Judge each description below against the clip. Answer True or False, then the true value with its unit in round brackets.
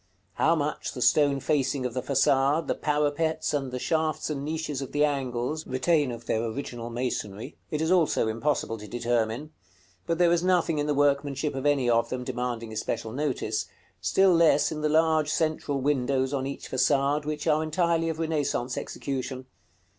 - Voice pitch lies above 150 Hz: False (140 Hz)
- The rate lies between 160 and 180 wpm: True (175 wpm)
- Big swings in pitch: False (3.5 semitones)